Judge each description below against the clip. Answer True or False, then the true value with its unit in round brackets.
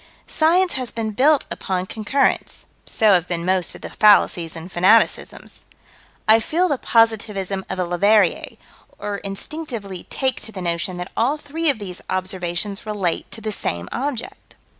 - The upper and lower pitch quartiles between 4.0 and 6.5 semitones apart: True (4.9 semitones)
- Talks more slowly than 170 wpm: True (160 wpm)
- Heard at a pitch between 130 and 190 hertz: False (205 Hz)